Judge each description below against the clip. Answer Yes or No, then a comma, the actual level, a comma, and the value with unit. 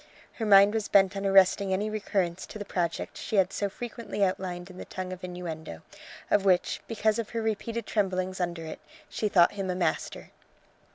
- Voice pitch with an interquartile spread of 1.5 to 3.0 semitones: Yes, narrow, 2.5 semitones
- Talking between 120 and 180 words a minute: No, average, 190 wpm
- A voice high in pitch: Yes, high, 195 Hz